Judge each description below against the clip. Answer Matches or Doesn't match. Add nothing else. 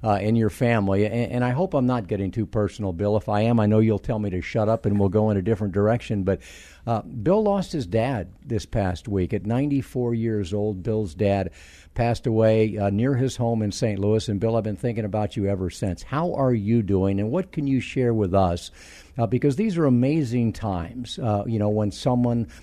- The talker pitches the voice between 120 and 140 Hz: Doesn't match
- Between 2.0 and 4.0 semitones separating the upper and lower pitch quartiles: Matches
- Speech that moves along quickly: Matches